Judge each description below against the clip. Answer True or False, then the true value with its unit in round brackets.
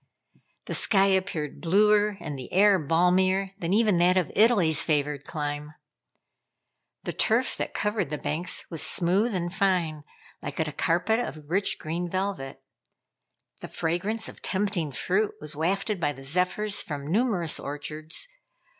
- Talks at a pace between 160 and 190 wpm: False (145 wpm)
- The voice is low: False (175 Hz)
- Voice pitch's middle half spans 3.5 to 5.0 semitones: True (4.5 semitones)